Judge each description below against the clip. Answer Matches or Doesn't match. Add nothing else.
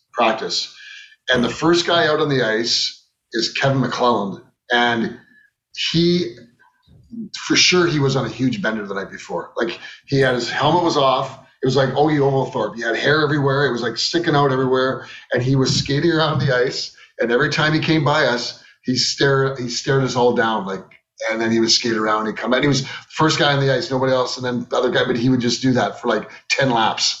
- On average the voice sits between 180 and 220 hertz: Doesn't match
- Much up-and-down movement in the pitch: Doesn't match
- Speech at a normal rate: Doesn't match